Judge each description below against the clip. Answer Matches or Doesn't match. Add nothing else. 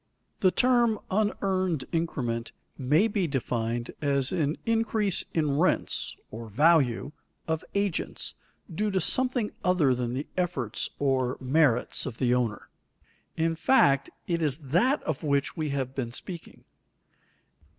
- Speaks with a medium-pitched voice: Matches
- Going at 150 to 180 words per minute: Doesn't match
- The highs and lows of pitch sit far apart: Matches